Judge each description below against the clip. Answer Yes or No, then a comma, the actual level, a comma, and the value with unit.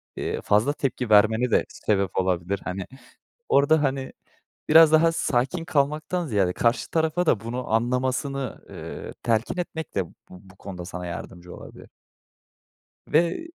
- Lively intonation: Yes, wide, 7.6 semitones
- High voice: No, low, 125 Hz